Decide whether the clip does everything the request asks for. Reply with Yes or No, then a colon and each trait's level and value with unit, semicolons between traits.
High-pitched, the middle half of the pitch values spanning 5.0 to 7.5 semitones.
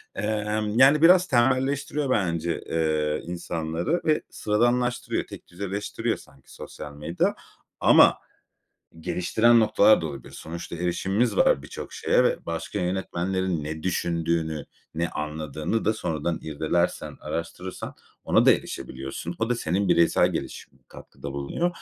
No: very low, 90 Hz; wide, 5.4 semitones